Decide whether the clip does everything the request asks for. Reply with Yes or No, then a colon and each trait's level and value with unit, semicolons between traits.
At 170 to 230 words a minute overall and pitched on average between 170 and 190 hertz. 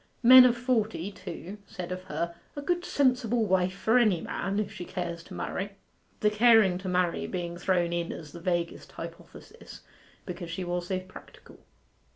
Yes: average, 175 wpm; medium, 185 Hz